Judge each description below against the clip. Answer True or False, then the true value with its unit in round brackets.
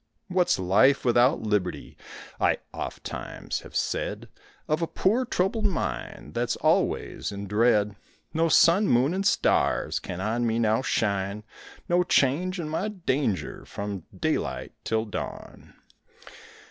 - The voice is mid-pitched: False (125 Hz)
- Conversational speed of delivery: False (130 wpm)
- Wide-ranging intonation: True (8.9 semitones)